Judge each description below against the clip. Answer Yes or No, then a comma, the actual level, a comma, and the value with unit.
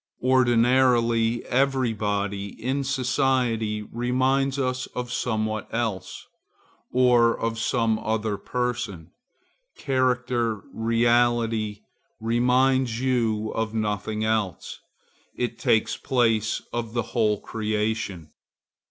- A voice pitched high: No, low, 115 Hz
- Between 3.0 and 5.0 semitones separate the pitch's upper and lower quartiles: No, narrow, 2.4 semitones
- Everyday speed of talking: No, slow, 90 wpm